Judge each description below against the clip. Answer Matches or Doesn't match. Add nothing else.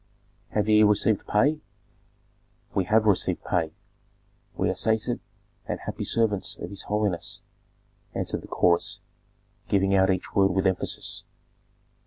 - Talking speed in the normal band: Doesn't match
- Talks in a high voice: Doesn't match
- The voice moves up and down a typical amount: Doesn't match